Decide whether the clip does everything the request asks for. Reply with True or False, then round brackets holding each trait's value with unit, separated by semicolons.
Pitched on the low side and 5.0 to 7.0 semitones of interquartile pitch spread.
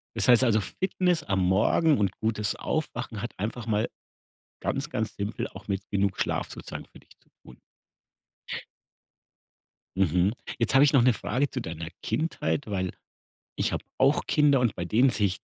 True (110 Hz; 5.5 semitones)